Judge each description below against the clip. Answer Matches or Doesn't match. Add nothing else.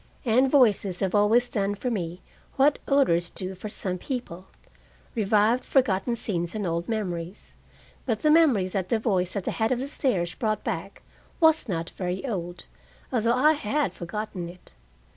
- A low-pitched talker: Doesn't match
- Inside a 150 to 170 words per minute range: Matches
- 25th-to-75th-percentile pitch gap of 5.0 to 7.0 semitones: Matches